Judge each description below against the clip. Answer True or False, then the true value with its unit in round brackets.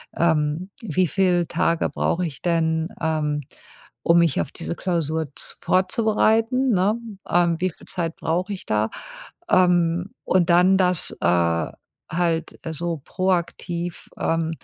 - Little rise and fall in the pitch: True (2.3 semitones)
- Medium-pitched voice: True (170 Hz)